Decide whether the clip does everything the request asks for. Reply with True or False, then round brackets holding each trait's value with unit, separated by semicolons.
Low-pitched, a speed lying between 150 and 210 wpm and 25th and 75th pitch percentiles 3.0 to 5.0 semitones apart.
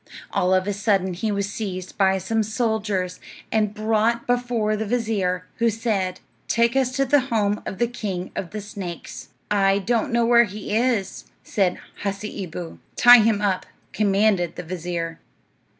False (210 Hz; 160 wpm; 3.3 semitones)